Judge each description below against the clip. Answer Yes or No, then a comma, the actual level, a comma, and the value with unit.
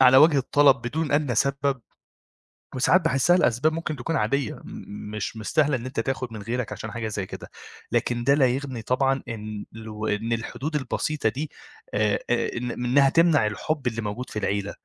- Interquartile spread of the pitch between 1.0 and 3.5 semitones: No, average, 4.3 semitones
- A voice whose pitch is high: No, low, 125 Hz